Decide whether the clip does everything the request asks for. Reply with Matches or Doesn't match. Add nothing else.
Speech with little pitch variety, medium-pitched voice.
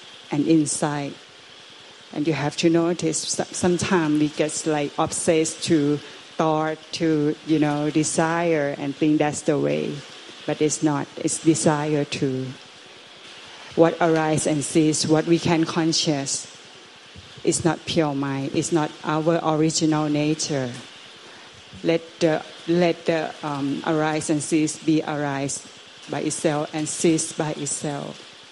Matches